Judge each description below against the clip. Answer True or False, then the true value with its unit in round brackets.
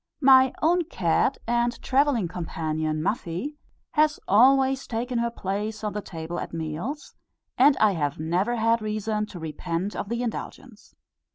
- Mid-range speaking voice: False (215 Hz)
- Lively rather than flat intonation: True (6.9 semitones)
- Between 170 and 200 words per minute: False (150 wpm)